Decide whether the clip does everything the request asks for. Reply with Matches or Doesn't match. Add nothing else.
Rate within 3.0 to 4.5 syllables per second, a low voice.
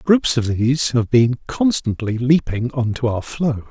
Matches